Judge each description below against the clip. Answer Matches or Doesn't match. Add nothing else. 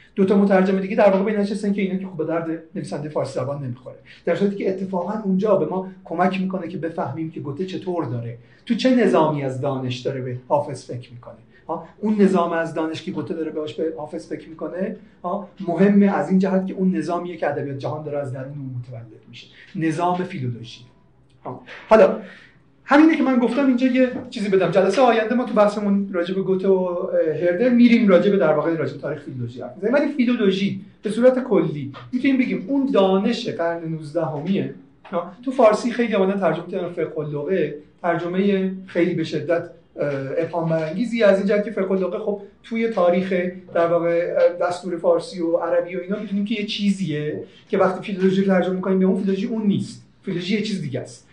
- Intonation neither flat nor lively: Matches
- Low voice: Doesn't match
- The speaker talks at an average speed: Doesn't match